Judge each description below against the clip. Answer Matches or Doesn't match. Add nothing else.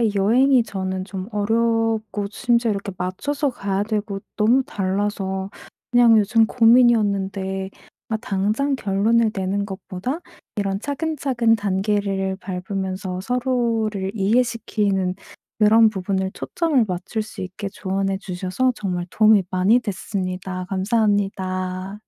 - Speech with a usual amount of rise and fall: Matches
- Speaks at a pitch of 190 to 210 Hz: Matches